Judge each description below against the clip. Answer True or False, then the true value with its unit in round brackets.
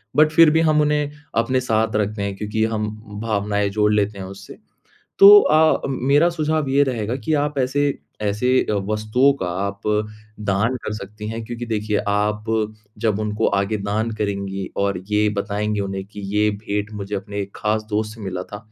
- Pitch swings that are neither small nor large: True (3.6 semitones)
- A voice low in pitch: True (105 Hz)